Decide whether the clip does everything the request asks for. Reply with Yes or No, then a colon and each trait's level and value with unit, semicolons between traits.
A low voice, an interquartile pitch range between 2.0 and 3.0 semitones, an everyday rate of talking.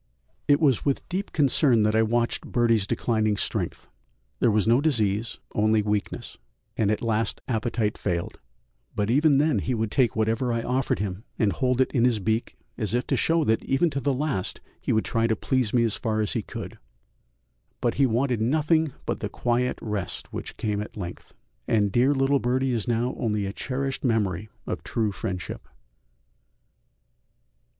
No: low, 115 Hz; average, 3.5 semitones; average, 180 wpm